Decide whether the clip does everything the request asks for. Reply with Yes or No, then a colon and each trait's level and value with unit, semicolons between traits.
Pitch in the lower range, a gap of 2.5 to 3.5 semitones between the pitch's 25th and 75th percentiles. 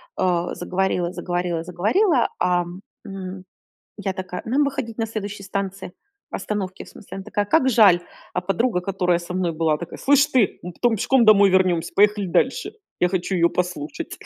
No: high, 190 Hz; average, 3.0 semitones